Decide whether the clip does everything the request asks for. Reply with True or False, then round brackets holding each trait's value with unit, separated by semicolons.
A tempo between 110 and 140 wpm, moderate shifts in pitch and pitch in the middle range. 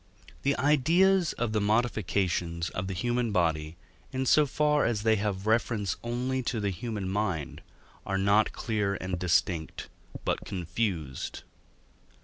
False (135 wpm; 4.8 semitones; 105 Hz)